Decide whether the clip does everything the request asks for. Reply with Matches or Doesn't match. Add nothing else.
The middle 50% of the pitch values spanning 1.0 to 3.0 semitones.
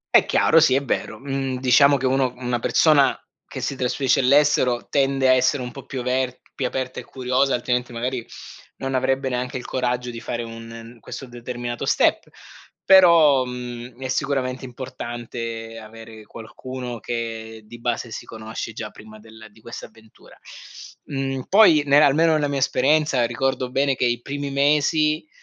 Matches